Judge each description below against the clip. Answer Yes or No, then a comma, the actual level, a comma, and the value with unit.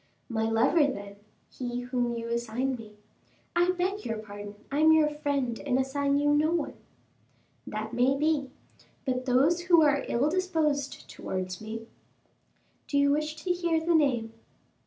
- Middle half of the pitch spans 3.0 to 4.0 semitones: No, average, 4.8 semitones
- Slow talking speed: No, average, 160 wpm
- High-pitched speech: Yes, very high, 275 Hz